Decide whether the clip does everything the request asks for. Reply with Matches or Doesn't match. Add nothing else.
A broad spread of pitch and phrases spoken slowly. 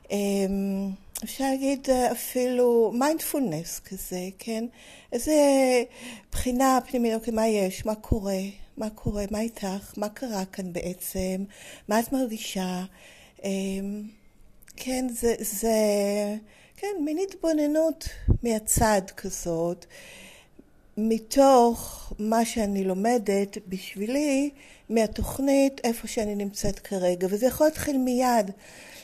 Doesn't match